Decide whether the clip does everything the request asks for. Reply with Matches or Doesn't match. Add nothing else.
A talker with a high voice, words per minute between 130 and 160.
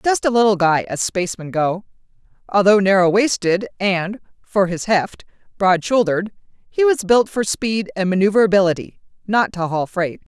Matches